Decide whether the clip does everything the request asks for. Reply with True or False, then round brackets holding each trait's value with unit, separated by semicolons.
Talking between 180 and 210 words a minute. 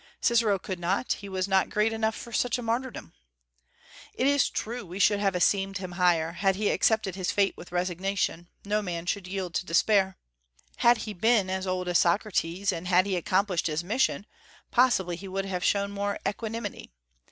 True (185 wpm)